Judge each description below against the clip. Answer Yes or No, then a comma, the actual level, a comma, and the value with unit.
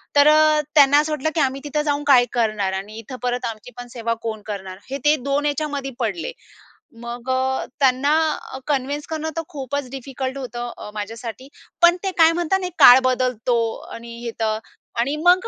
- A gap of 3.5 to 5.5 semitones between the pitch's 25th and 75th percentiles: Yes, average, 4.0 semitones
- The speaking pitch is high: Yes, very high, 265 Hz